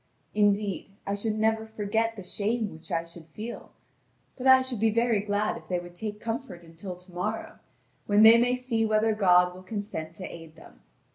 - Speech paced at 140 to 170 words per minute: No, average, 195 wpm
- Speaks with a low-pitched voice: No, high, 210 Hz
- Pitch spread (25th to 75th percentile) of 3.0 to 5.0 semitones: Yes, average, 3.8 semitones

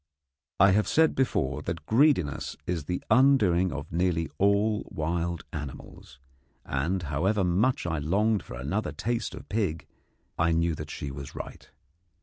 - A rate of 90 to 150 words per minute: Yes, average, 145 wpm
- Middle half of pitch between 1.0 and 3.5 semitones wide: No, wide, 5.4 semitones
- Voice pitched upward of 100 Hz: No, very low, 85 Hz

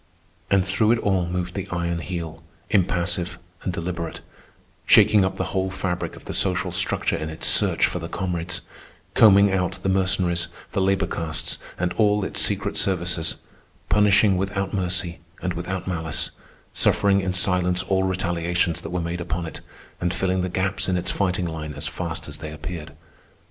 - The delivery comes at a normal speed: Yes, average, 170 wpm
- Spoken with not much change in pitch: Yes, narrow, 1.9 semitones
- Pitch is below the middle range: Yes, very low, 90 Hz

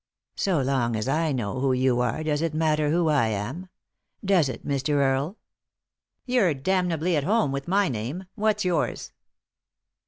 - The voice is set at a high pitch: No, medium, 150 Hz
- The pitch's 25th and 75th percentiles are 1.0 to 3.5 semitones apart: No, average, 5.2 semitones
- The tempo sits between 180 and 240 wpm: Yes, average, 185 wpm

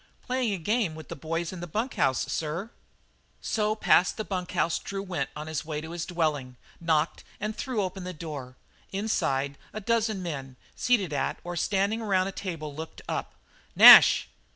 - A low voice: No, medium, 175 Hz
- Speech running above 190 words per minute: No, average, 180 wpm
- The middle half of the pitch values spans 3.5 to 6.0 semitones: Yes, average, 4.9 semitones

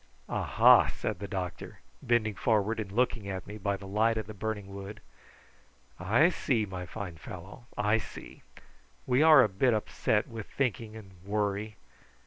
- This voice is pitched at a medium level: No, low, 105 Hz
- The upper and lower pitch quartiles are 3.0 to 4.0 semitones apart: No, narrow, 2.5 semitones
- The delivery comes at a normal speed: Yes, average, 160 wpm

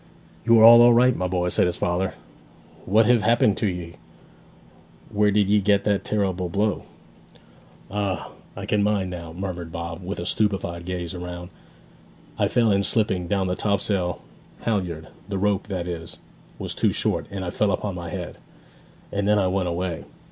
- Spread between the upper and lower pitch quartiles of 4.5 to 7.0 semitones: No, average, 2.8 semitones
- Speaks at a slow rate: No, average, 175 wpm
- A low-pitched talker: Yes, very low, 95 Hz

